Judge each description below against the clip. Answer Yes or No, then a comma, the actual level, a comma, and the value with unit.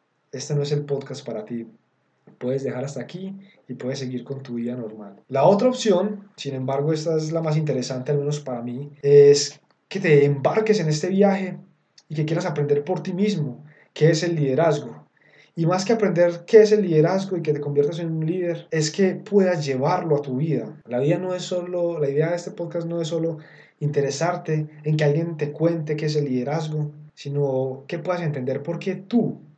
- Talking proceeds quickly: Yes, fast, 210 wpm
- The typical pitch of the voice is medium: Yes, medium, 155 Hz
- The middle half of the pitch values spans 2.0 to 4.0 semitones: Yes, average, 3.7 semitones